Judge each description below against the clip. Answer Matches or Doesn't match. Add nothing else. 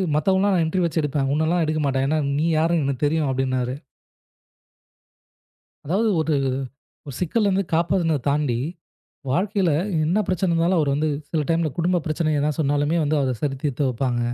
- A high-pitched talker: Doesn't match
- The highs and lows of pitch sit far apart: Doesn't match